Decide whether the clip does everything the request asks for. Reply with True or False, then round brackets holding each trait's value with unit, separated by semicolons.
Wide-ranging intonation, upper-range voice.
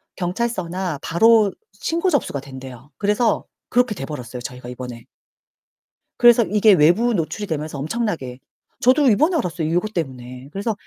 False (8.8 semitones; 180 Hz)